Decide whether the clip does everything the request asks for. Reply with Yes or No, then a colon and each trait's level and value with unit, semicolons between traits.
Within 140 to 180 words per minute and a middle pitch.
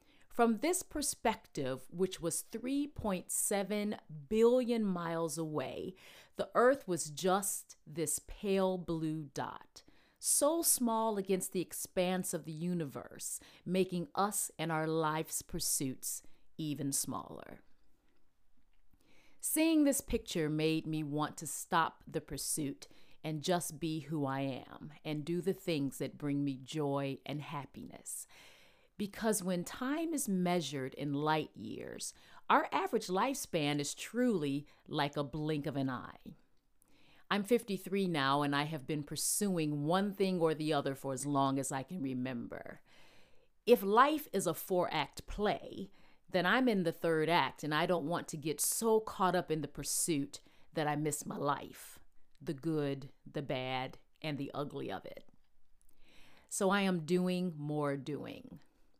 Yes: average, 145 wpm; medium, 165 Hz